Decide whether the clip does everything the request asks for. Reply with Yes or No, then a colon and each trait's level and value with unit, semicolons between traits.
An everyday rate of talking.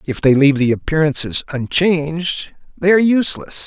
Yes: average, 150 wpm